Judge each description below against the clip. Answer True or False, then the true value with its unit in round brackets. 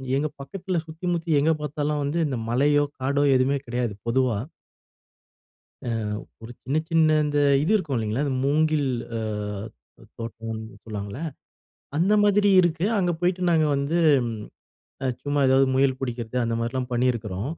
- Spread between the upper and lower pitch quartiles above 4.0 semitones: True (4.6 semitones)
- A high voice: False (140 Hz)